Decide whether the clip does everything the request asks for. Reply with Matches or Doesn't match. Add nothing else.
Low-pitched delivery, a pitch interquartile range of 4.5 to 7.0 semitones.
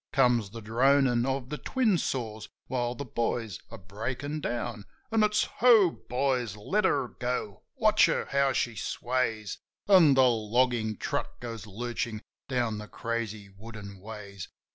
Doesn't match